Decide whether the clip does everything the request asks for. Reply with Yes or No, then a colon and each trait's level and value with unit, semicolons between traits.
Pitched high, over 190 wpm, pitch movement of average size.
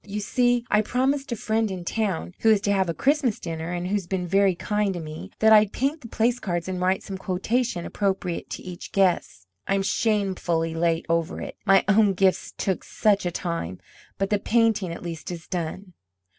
Yes: high, 195 Hz; average, 200 wpm; average, 3.7 semitones